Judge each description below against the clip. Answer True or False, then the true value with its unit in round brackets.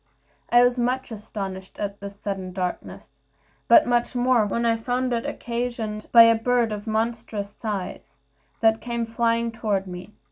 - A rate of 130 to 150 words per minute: False (165 wpm)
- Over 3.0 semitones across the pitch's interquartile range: False (2.7 semitones)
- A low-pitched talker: False (225 Hz)